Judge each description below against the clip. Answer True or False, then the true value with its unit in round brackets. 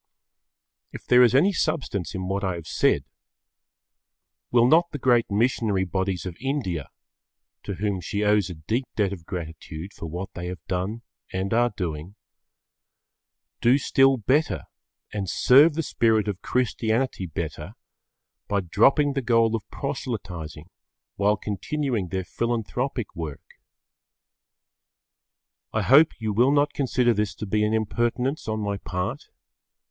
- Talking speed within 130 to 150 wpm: True (140 wpm)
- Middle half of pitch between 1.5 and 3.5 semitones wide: False (4.9 semitones)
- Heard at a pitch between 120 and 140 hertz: False (105 Hz)